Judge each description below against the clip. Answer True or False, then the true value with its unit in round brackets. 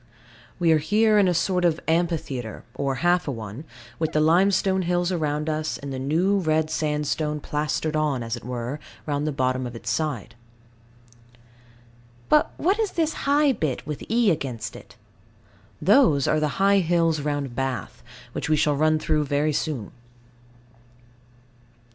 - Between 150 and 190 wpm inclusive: True (155 wpm)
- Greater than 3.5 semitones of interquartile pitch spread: True (4.0 semitones)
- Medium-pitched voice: True (155 Hz)